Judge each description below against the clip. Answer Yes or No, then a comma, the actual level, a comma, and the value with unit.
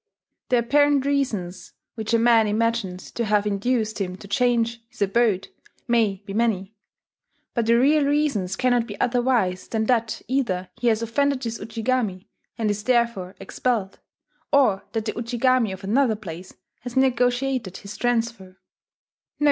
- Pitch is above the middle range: Yes, high, 230 Hz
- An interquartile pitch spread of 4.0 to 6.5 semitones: No, average, 3.5 semitones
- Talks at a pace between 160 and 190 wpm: No, average, 150 wpm